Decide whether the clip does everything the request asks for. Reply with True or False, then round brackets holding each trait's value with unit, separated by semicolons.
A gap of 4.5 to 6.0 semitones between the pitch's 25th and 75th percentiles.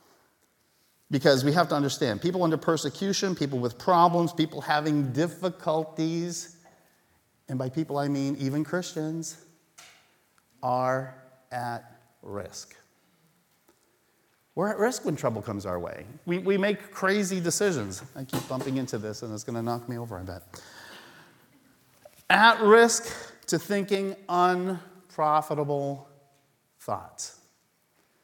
True (5.4 semitones)